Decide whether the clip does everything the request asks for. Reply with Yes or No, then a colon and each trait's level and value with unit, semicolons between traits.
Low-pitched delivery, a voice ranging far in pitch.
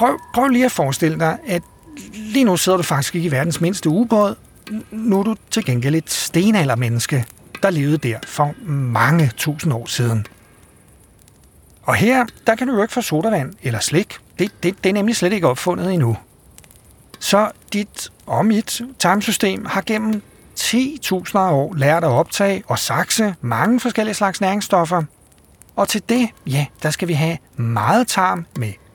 No: medium, 180 Hz; wide, 6.7 semitones